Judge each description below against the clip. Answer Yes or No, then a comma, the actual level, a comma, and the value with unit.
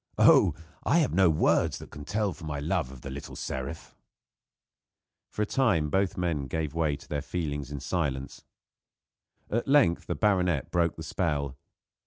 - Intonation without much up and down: No, average, 4.2 semitones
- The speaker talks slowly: No, average, 170 wpm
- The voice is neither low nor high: No, very low, 80 Hz